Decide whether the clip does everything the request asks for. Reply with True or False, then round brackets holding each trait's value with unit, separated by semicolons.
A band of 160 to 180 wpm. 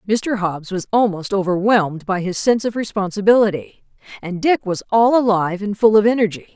True (175 wpm)